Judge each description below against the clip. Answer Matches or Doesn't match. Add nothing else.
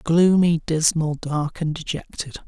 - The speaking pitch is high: Doesn't match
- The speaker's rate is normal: Doesn't match